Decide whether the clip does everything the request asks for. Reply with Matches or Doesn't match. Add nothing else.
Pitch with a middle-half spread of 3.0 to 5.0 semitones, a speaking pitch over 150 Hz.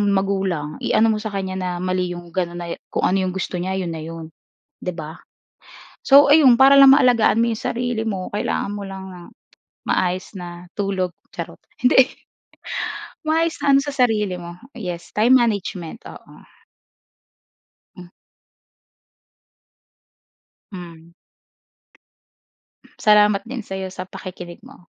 Matches